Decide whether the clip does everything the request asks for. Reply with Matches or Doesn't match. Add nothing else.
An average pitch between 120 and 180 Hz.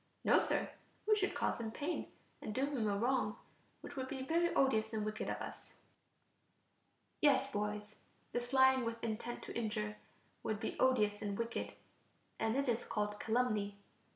Doesn't match